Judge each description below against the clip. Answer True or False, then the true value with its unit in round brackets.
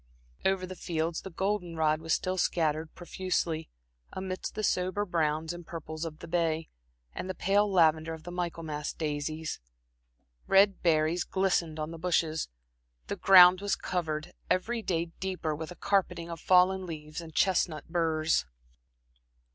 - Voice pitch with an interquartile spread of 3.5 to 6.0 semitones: False (2.7 semitones)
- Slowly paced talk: False (150 wpm)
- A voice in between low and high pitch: True (170 Hz)